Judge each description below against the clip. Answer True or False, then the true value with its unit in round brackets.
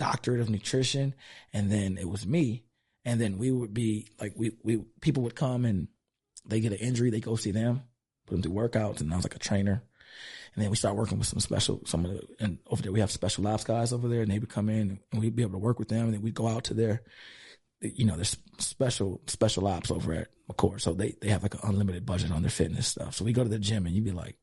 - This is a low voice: True (110 Hz)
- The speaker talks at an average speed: False (270 wpm)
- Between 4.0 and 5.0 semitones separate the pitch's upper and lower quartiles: False (2.8 semitones)